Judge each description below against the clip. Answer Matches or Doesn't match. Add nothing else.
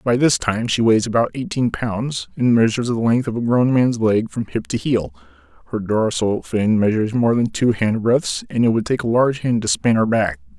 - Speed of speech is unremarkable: Doesn't match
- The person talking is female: Doesn't match